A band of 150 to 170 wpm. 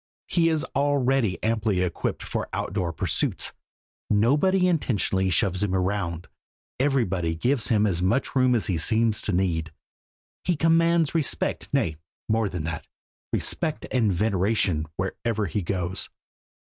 No: slow, 135 wpm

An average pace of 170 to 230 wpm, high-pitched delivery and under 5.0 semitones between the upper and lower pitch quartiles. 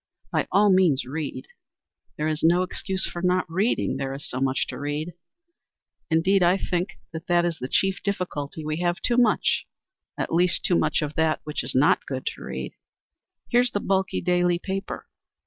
No: average, 180 wpm; medium, 175 Hz; average, 3.8 semitones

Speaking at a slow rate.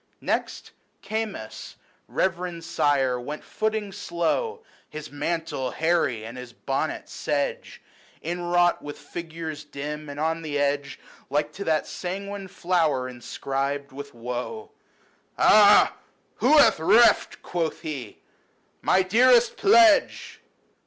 Yes: slow, 125 wpm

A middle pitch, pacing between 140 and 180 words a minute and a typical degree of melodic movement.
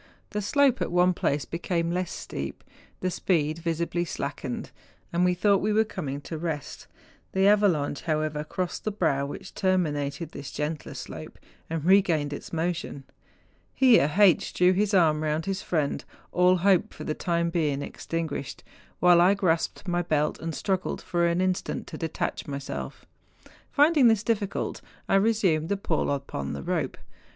Yes: medium, 170 Hz; average, 160 wpm; average, 3.9 semitones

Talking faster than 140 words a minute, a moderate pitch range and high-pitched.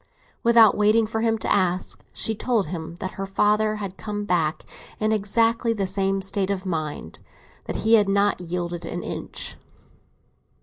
Yes: average, 160 wpm; average, 3.1 semitones; high, 200 Hz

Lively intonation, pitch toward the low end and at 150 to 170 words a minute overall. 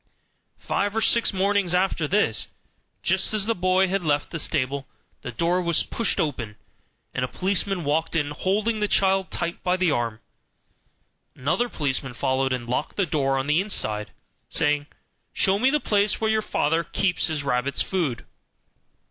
No: wide, 5.8 semitones; medium, 170 Hz; average, 165 wpm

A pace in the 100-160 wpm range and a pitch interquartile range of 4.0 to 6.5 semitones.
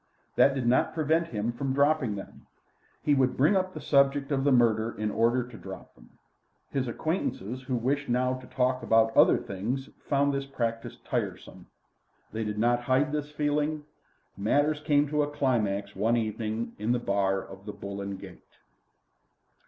No: average, 175 wpm; average, 4.4 semitones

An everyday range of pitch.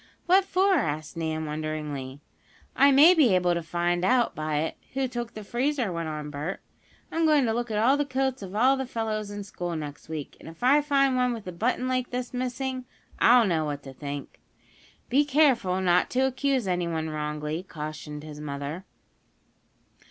No: wide, 8.7 semitones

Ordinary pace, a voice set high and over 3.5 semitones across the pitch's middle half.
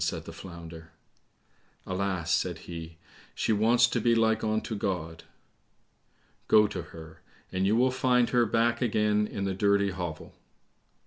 No: average, 145 wpm; low, 100 Hz; average, 4.5 semitones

